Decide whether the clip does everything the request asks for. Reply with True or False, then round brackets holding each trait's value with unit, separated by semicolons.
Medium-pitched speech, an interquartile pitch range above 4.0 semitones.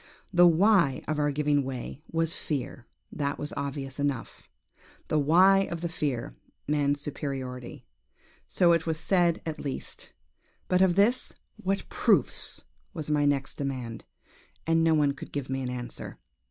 False (150 Hz; 3.4 semitones)